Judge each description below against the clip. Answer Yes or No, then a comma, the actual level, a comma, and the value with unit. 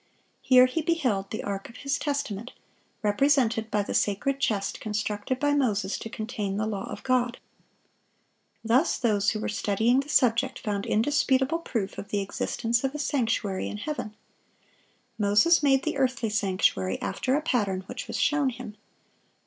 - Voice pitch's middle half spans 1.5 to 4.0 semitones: No, average, 4.7 semitones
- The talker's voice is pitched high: Yes, high, 230 Hz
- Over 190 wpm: No, average, 160 wpm